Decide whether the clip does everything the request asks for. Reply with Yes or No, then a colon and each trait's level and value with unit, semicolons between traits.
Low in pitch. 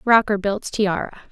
No: high, 205 Hz